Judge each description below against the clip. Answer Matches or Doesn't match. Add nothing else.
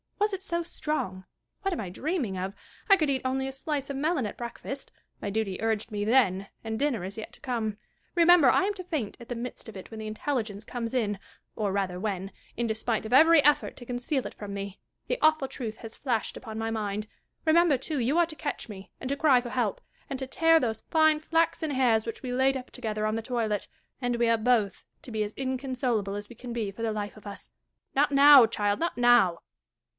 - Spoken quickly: Matches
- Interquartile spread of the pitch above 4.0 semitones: Matches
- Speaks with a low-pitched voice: Doesn't match